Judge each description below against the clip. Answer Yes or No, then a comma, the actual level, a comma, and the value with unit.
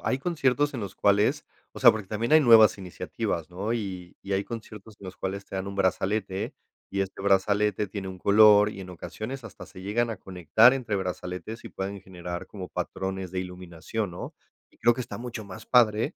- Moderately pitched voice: No, low, 100 Hz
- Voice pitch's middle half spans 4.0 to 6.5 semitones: No, average, 2.8 semitones